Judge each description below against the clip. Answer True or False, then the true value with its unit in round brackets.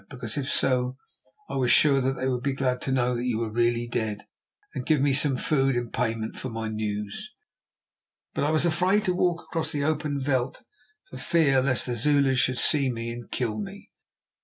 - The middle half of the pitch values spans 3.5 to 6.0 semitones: False (3.1 semitones)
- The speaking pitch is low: True (130 Hz)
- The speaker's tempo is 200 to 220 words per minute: True (205 wpm)